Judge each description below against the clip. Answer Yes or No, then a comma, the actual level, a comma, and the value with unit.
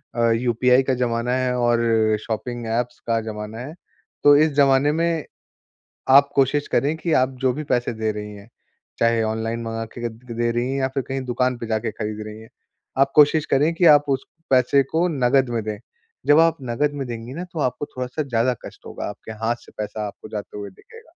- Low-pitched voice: Yes, low, 125 Hz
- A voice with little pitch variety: No, average, 3.6 semitones